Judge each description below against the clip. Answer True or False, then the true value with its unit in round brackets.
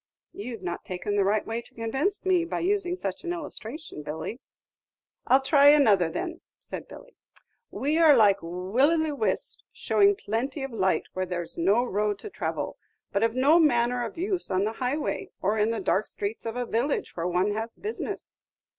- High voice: True (235 Hz)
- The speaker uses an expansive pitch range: True (7.3 semitones)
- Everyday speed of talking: True (190 wpm)